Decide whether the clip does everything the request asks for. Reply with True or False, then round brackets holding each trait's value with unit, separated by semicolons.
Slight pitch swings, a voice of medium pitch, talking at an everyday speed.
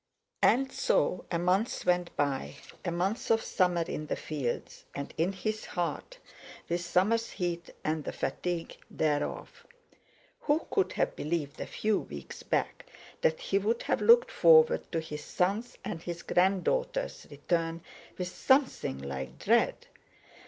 False (5.4 semitones; 175 Hz; 145 wpm)